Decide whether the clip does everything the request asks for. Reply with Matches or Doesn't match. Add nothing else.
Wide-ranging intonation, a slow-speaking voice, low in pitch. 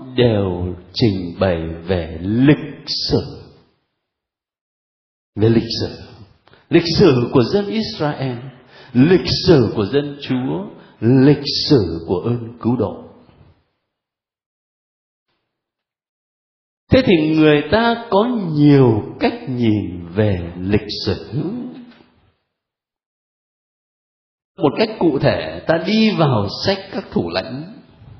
Matches